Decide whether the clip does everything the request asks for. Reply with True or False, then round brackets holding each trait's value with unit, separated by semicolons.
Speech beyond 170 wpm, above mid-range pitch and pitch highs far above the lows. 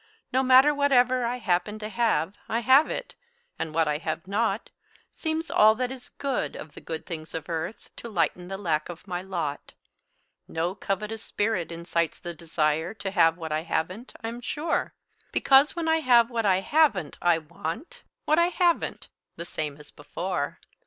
True (180 wpm; 195 Hz; 7.2 semitones)